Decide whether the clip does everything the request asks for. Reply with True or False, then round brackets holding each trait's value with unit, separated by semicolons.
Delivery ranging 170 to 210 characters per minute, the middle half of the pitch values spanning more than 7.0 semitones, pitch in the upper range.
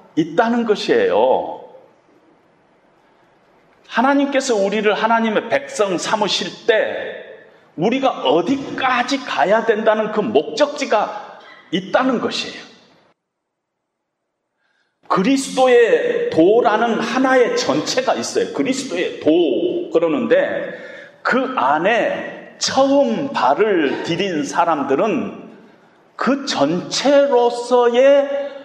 True (200 characters per minute; 8.2 semitones; 270 Hz)